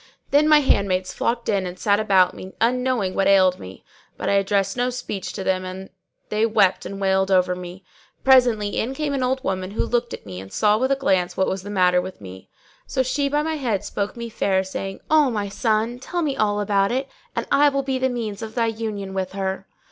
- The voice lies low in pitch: No, high, 205 Hz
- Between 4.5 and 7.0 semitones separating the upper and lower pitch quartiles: Yes, average, 4.8 semitones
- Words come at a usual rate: No, fast, 240 wpm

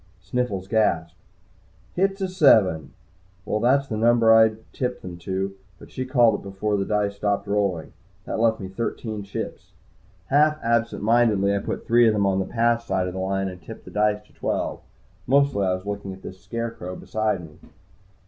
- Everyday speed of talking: Yes, average, 185 wpm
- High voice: No, low, 105 Hz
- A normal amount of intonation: Yes, average, 3.4 semitones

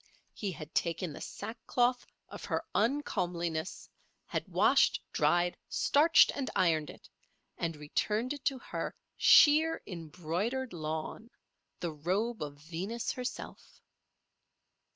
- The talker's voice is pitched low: No, medium, 185 Hz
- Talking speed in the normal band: No, slow, 110 wpm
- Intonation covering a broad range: Yes, wide, 7.1 semitones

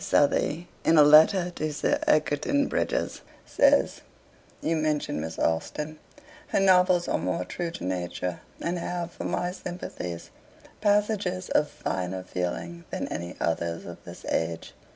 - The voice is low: No, medium, 155 Hz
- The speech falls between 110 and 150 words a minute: Yes, average, 140 wpm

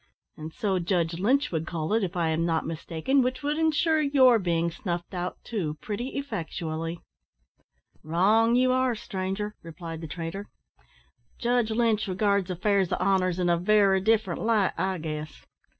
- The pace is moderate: Yes, average, 160 wpm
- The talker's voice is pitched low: No, high, 190 Hz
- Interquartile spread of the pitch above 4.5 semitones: Yes, average, 5.2 semitones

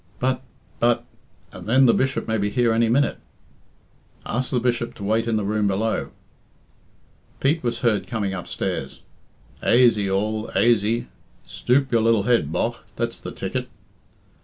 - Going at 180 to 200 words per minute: No, average, 150 wpm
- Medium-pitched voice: No, low, 115 Hz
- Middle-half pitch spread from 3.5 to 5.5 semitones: No, narrow, 2.5 semitones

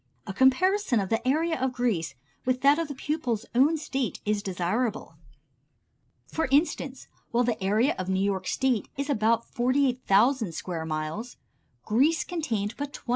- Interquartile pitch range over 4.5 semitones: Yes, average, 5.3 semitones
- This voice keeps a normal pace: Yes, average, 155 wpm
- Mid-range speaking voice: No, high, 245 Hz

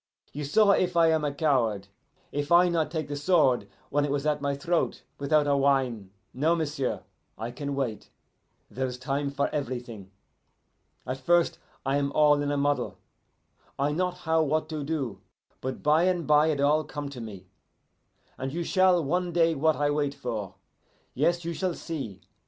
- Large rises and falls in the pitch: No, average, 3.0 semitones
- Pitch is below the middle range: No, medium, 145 Hz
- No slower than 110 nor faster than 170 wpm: No, average, 180 wpm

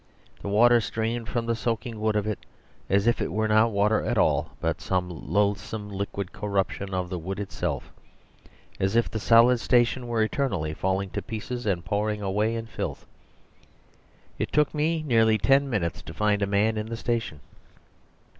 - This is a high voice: No, low, 110 Hz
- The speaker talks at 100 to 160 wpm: No, average, 175 wpm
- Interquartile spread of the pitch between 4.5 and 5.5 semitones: No, average, 2.7 semitones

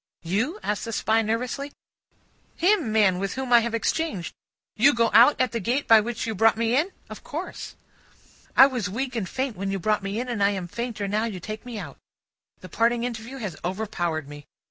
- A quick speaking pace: Yes, fast, 210 wpm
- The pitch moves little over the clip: No, average, 3.7 semitones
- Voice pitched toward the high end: Yes, high, 225 Hz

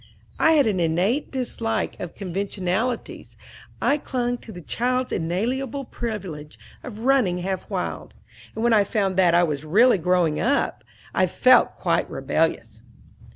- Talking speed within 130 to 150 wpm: Yes, average, 145 wpm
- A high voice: Yes, high, 205 Hz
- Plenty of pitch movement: Yes, wide, 5.8 semitones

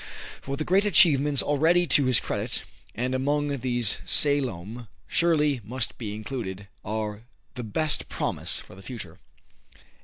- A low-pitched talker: Yes, low, 130 Hz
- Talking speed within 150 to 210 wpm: No, slow, 135 wpm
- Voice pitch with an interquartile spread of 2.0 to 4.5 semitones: No, average, 5.1 semitones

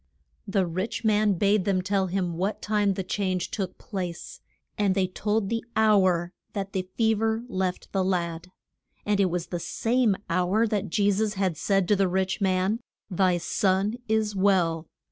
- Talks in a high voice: Yes, high, 195 Hz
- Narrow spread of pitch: Yes, narrow, 2.3 semitones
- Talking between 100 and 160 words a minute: No, average, 175 wpm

